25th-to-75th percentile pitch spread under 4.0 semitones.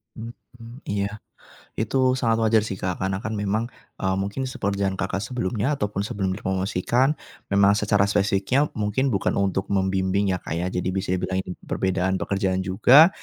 Yes: average, 2.8 semitones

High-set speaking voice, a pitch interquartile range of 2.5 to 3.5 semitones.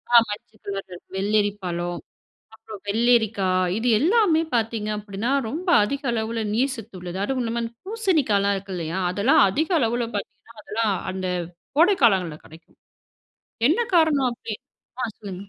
No: high, 220 Hz; average, 4.0 semitones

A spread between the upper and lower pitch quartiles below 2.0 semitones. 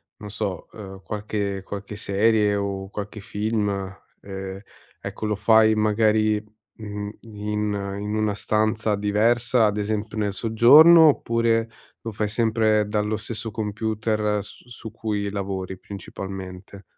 Yes: narrow, 1.4 semitones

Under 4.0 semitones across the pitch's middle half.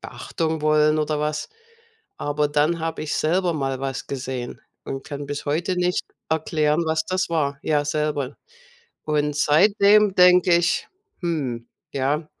Yes: narrow, 2.6 semitones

